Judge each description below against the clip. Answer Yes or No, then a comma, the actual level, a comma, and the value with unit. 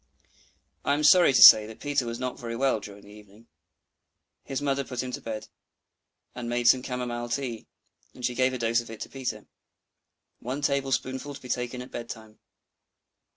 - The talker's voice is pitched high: No, low, 125 Hz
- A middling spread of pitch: No, narrow, 2.3 semitones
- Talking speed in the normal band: Yes, average, 190 wpm